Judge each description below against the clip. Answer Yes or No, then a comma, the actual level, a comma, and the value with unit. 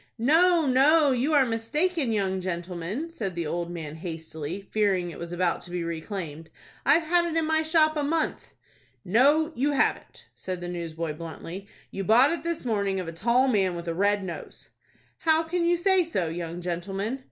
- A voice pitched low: No, high, 200 Hz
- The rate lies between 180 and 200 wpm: Yes, average, 185 wpm